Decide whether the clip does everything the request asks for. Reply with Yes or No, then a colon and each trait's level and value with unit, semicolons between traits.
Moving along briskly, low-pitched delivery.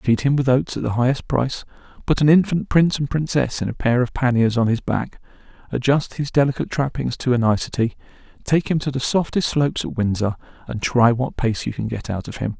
Yes: fast, 225 wpm; low, 130 Hz